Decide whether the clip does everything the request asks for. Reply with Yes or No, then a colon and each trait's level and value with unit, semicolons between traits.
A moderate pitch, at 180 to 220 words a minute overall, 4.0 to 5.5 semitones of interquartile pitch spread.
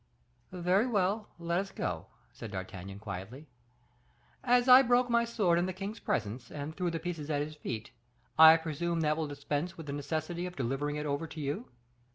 Yes: medium, 160 Hz; average, 190 wpm; average, 4.4 semitones